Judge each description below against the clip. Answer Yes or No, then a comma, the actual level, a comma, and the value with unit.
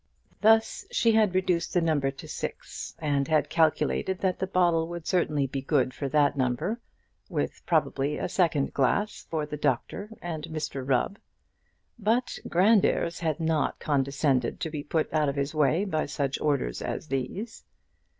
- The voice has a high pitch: No, medium, 155 Hz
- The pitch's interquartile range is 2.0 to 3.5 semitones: No, average, 4.3 semitones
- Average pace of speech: Yes, average, 160 wpm